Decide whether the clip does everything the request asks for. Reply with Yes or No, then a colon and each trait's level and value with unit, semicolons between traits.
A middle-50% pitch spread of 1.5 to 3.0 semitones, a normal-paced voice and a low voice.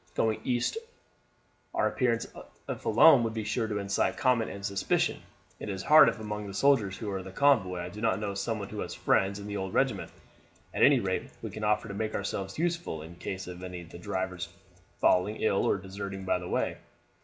No: narrow, 2.6 semitones; fast, 210 wpm; low, 100 Hz